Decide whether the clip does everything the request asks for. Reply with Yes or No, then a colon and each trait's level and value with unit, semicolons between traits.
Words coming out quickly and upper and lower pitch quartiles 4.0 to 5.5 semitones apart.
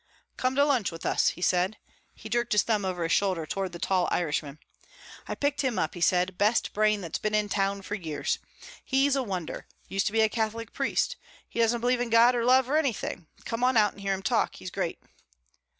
Yes: fast, 225 wpm; average, 4.5 semitones